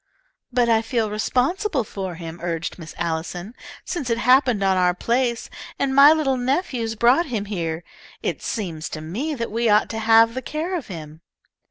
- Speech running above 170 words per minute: Yes, average, 180 wpm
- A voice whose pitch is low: No, high, 225 Hz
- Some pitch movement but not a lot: No, wide, 6.2 semitones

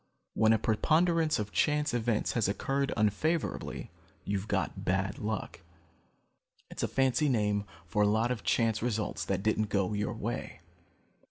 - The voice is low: Yes, low, 110 Hz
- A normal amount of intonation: Yes, average, 4.1 semitones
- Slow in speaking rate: No, average, 150 wpm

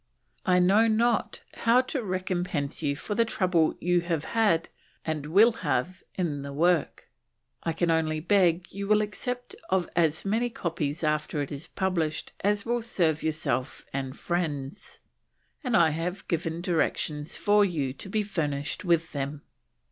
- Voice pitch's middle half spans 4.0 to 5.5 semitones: Yes, average, 4.7 semitones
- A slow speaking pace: No, average, 155 wpm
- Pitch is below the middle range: No, medium, 170 Hz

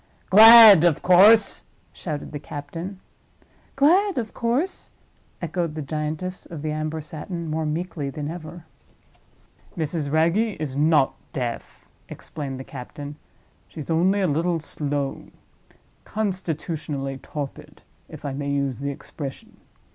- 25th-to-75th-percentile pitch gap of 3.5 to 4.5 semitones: Yes, average, 4.1 semitones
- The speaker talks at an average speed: No, slow, 120 wpm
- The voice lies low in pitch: No, medium, 155 Hz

